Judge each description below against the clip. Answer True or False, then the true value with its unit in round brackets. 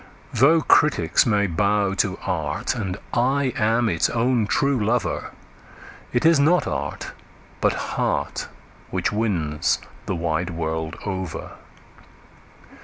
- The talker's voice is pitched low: True (105 Hz)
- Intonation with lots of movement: True (6.2 semitones)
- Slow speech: True (115 wpm)